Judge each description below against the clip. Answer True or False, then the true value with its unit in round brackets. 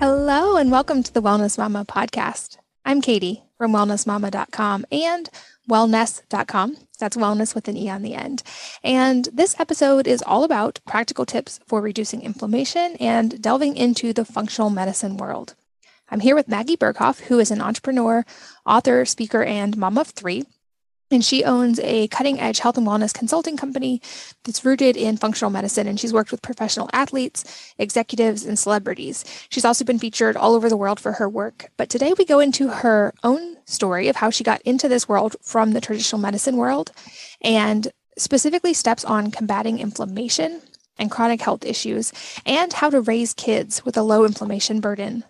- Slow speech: False (175 wpm)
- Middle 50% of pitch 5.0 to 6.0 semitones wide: False (3.6 semitones)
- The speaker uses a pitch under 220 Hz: False (230 Hz)